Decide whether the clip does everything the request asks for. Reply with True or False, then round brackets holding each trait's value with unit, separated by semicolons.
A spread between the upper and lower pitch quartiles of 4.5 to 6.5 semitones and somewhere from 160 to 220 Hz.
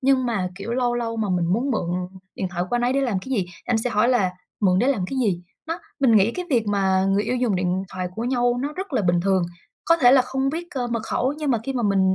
False (5.2 semitones; 235 Hz)